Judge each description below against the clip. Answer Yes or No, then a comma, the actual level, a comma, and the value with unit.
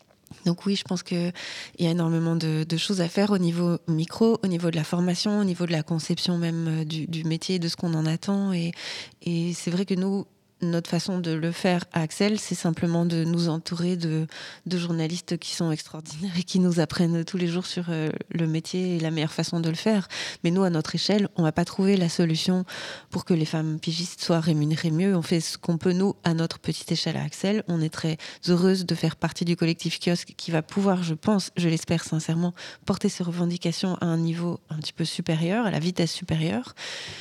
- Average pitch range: No, narrow, 2.0 semitones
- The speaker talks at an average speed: No, fast, 225 wpm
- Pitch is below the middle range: No, medium, 170 Hz